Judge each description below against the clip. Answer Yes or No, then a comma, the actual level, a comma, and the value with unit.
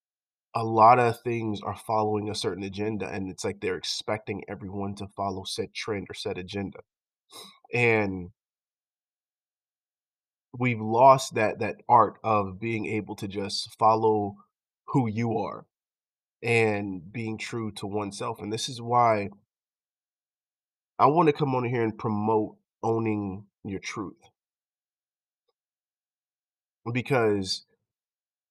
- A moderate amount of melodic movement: No, narrow, 2.3 semitones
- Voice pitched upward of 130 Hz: No, low, 110 Hz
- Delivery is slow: Yes, slow, 120 wpm